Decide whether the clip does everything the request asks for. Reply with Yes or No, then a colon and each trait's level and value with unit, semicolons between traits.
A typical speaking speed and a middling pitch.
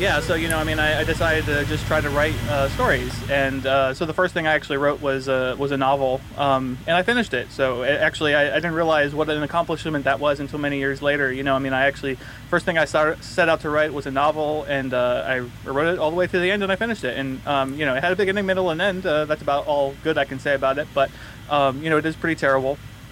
No: fast, 290 wpm; medium, 145 Hz